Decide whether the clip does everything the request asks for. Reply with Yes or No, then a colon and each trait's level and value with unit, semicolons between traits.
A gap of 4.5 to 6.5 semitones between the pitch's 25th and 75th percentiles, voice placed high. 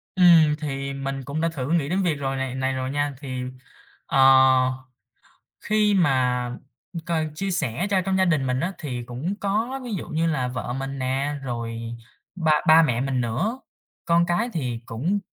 No: average, 4.9 semitones; medium, 145 Hz